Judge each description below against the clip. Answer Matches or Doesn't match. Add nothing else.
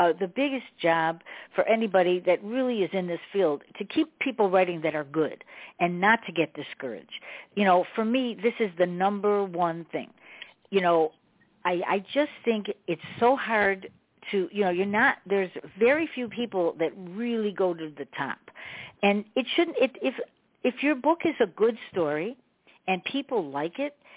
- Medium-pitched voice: Doesn't match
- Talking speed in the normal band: Matches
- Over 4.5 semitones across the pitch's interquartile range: Matches